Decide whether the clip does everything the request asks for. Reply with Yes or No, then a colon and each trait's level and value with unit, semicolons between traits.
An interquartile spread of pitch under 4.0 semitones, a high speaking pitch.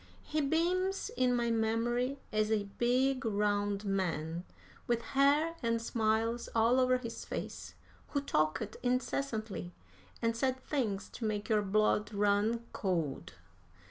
Yes: average, 3.6 semitones; high, 230 Hz